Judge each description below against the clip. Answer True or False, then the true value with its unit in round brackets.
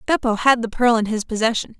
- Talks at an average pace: False (235 wpm)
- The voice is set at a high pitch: True (230 Hz)